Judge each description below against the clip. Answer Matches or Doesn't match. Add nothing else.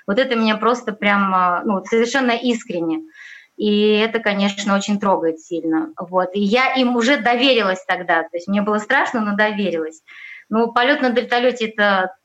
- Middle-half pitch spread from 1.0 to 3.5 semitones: Doesn't match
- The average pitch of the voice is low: Doesn't match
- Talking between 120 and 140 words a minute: Doesn't match